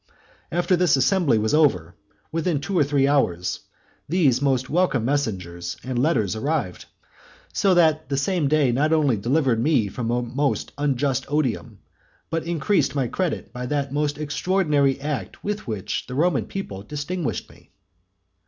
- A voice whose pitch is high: No, medium, 140 Hz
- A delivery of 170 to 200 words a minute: No, average, 155 wpm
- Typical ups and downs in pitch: Yes, average, 4.4 semitones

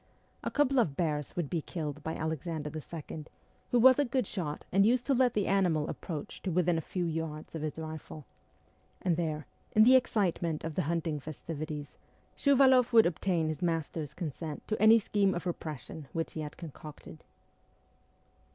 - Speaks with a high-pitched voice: No, medium, 165 Hz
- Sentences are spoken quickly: No, average, 175 wpm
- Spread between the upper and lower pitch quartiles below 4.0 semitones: No, average, 4.3 semitones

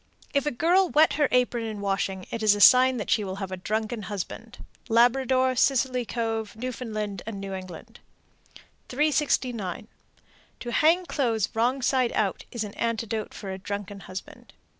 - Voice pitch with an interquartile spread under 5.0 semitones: Yes, average, 3.9 semitones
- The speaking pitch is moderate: No, high, 230 Hz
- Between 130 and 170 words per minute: Yes, average, 160 wpm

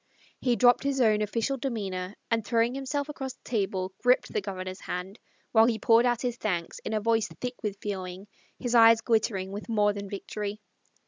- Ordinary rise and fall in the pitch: Yes, average, 3.4 semitones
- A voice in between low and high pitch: No, high, 220 Hz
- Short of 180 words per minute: No, average, 190 wpm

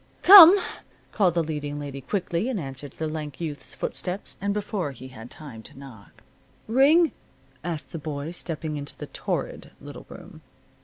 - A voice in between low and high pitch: Yes, medium, 155 Hz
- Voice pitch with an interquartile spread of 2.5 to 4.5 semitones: No, wide, 5.6 semitones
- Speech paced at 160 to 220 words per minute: Yes, average, 170 wpm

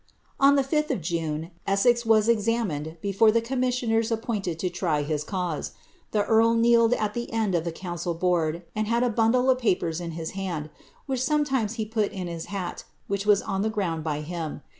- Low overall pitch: No, high, 205 Hz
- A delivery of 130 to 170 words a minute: No, average, 200 wpm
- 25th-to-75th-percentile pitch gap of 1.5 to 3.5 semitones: No, average, 5.3 semitones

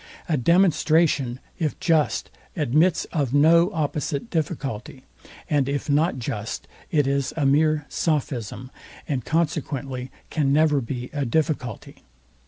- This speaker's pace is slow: Yes, slow, 120 wpm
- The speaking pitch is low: No, medium, 145 Hz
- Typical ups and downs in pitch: Yes, average, 3.2 semitones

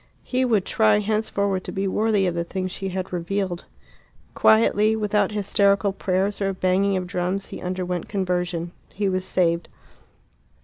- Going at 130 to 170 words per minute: Yes, average, 150 wpm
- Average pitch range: No, narrow, 2.0 semitones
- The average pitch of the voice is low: No, high, 190 Hz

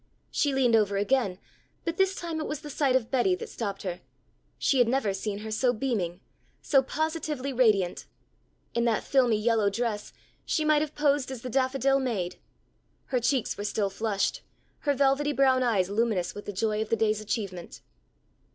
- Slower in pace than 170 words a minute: No, average, 180 wpm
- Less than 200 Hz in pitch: No, high, 240 Hz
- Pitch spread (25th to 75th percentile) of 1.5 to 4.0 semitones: No, average, 4.7 semitones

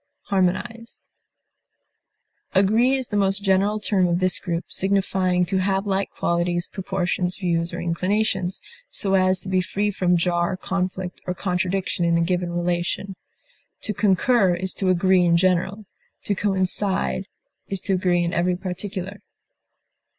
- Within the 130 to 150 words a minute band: Yes, average, 145 wpm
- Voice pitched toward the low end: No, medium, 185 Hz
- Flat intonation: Yes, narrow, 1.7 semitones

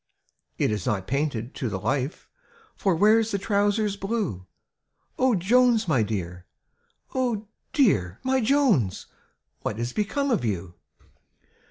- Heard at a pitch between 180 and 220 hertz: Yes, high, 190 Hz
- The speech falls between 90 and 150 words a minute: Yes, slow, 135 wpm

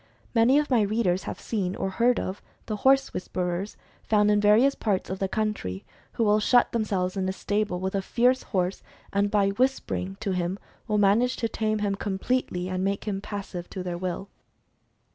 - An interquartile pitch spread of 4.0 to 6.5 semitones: No, average, 2.8 semitones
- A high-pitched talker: Yes, high, 205 Hz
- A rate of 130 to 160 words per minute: No, average, 195 wpm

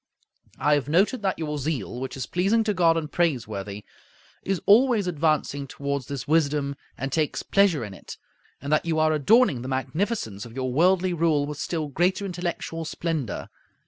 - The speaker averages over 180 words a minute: No, average, 175 wpm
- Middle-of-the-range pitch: Yes, medium, 155 Hz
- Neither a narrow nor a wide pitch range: Yes, average, 4.5 semitones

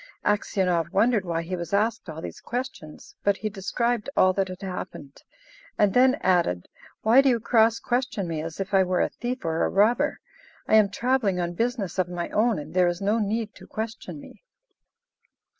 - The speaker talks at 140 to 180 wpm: No, average, 190 wpm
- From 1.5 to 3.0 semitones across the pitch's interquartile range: No, average, 4.5 semitones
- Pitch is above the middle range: Yes, high, 200 Hz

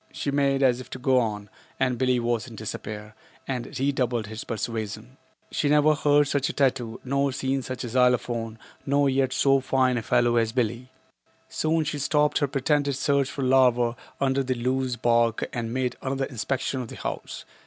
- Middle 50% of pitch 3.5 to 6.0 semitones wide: No, narrow, 2.5 semitones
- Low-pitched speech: Yes, low, 130 Hz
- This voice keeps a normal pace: Yes, average, 190 wpm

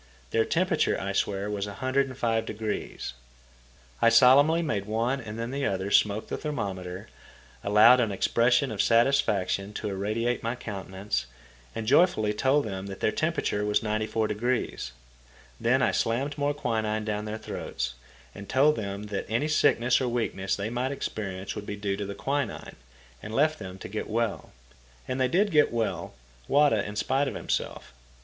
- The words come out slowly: No, average, 160 wpm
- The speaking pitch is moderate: No, low, 110 Hz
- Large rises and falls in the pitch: No, average, 4.1 semitones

